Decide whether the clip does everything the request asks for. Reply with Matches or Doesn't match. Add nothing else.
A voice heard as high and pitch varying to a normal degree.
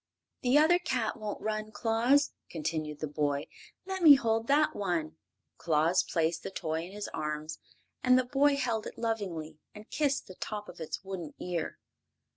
Doesn't match